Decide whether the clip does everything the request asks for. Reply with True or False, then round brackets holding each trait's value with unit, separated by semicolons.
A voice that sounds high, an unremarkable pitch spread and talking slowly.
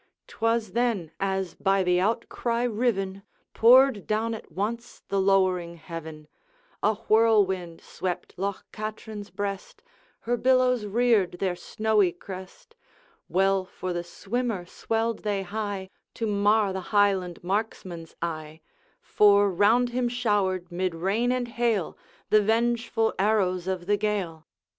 True (200 Hz; 3.4 semitones; 130 wpm)